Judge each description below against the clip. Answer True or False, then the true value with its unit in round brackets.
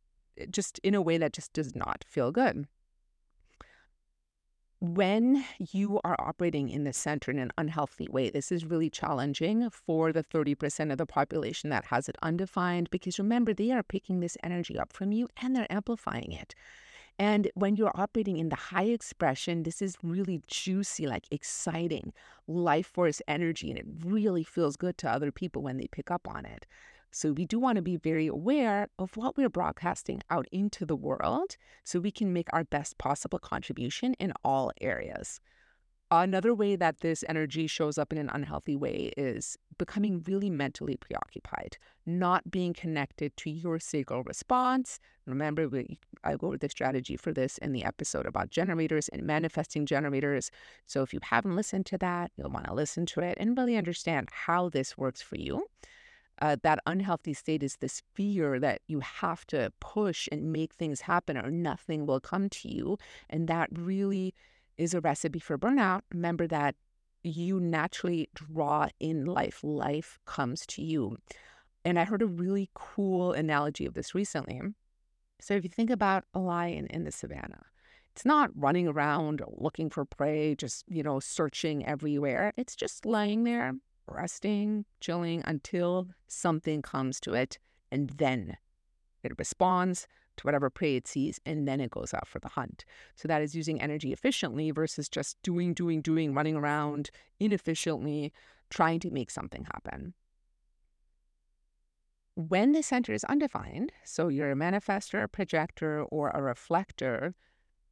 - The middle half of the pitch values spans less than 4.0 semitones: False (4.6 semitones)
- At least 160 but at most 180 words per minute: True (170 wpm)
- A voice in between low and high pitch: True (165 Hz)